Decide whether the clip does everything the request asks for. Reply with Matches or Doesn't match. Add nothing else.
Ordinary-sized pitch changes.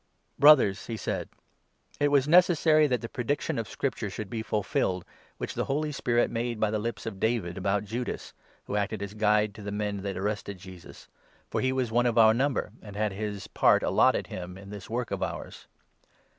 Matches